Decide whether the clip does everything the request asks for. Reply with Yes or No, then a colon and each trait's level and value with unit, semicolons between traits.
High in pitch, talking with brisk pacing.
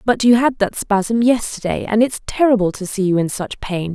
Yes: high, 215 Hz; fast, 245 wpm